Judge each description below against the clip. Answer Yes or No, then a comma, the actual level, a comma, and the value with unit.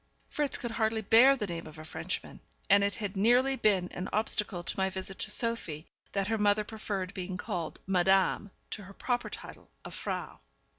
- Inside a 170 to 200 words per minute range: Yes, average, 190 wpm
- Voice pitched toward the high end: Yes, high, 200 Hz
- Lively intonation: No, average, 3.1 semitones